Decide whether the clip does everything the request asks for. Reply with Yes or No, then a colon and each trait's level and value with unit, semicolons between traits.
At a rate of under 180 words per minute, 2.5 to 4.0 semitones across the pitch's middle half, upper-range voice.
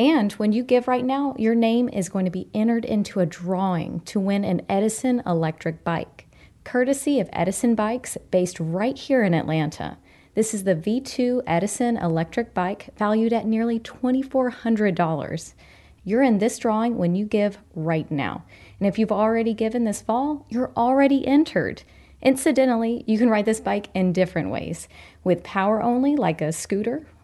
No: average, 165 wpm; average, 4.9 semitones; high, 220 Hz